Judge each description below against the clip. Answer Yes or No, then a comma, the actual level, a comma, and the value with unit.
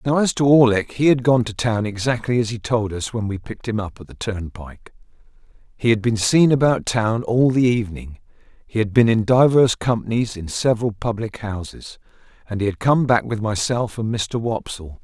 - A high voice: No, low, 110 Hz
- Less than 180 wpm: No, fast, 205 wpm